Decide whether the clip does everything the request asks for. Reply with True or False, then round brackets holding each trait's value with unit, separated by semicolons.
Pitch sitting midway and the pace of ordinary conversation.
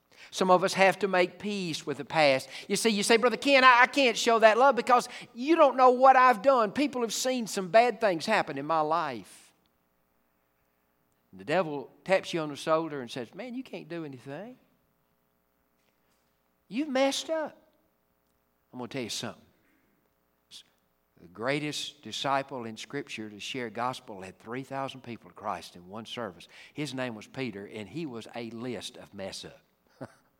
True (145 Hz; 180 wpm)